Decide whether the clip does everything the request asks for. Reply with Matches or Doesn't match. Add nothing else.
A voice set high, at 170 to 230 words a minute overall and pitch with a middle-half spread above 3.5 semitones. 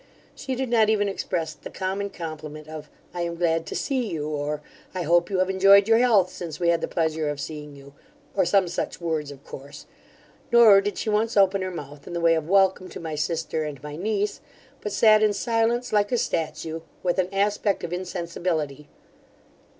Doesn't match